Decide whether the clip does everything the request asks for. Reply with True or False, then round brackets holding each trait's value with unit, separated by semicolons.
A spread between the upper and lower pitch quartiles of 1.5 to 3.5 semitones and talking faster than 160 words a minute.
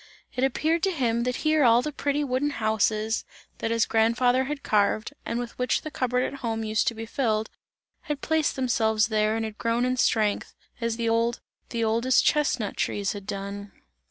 True (2.9 semitones; 195 wpm)